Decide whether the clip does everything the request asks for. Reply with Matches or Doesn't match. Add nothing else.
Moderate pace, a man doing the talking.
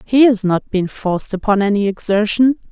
Doesn't match